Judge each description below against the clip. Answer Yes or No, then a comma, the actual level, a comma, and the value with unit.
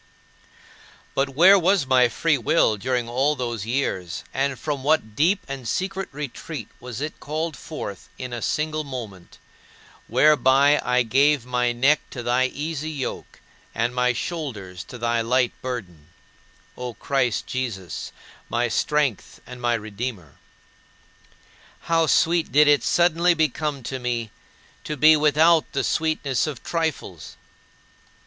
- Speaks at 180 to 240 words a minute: No, slow, 135 wpm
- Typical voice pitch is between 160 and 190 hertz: No, low, 130 Hz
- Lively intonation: No, average, 4.2 semitones